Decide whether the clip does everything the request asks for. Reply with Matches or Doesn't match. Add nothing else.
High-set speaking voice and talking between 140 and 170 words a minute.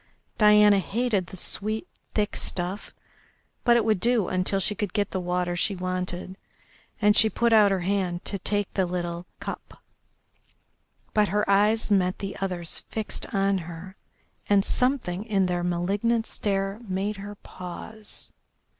Matches